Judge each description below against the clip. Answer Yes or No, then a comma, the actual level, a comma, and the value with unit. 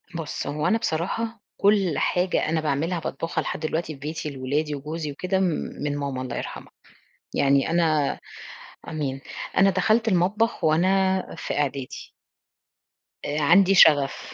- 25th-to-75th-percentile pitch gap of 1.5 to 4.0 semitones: No, average, 4.6 semitones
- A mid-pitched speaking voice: Yes, medium, 160 Hz